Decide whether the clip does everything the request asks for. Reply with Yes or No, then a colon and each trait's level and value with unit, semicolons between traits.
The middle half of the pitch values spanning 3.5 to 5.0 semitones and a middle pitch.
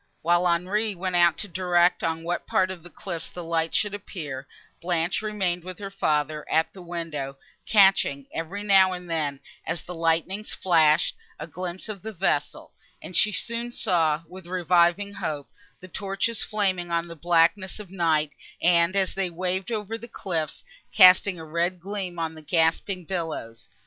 No: average, 2.8 semitones; medium, 175 Hz